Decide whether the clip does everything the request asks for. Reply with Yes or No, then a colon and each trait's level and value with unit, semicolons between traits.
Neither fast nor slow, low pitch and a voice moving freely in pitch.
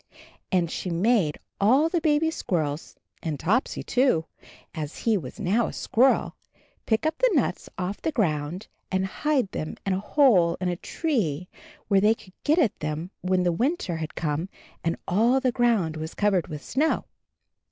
No: average, 175 wpm; high, 190 Hz; wide, 7.0 semitones